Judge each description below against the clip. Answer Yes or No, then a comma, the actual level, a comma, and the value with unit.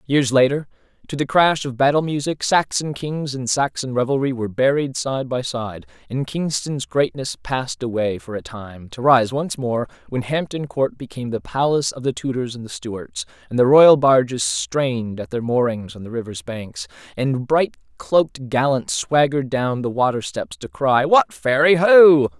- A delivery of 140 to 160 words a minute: No, average, 180 wpm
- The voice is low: Yes, low, 130 Hz